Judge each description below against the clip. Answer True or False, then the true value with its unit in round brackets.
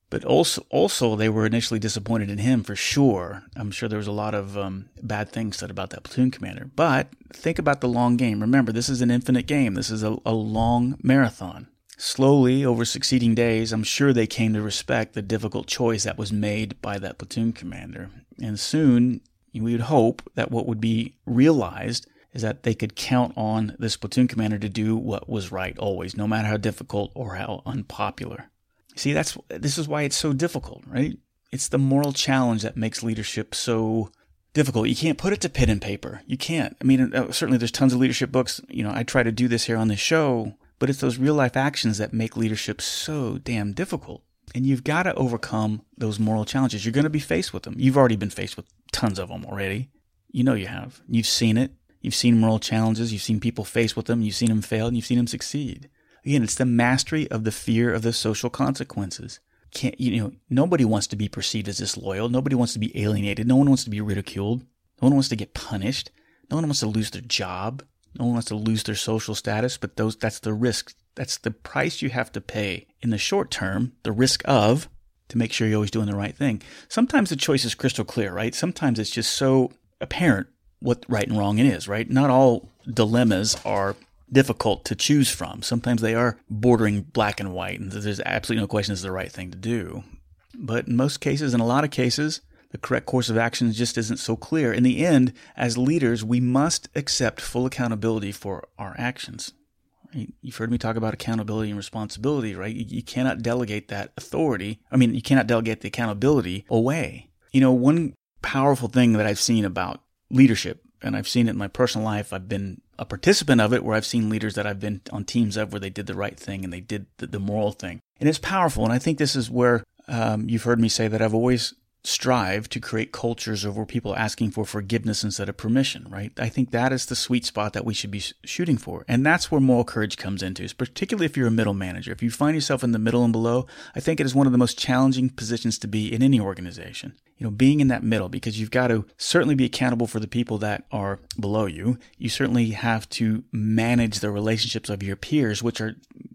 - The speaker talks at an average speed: False (225 wpm)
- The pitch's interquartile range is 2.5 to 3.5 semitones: True (3.2 semitones)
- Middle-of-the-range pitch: False (115 Hz)